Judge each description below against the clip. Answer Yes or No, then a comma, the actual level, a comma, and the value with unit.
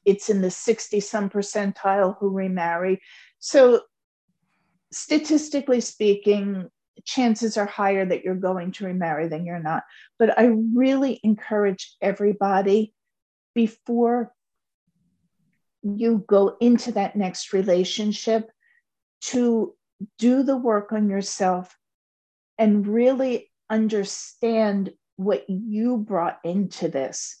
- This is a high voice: Yes, high, 205 Hz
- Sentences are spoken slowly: Yes, slow, 105 wpm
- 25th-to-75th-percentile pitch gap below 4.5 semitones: Yes, average, 3.4 semitones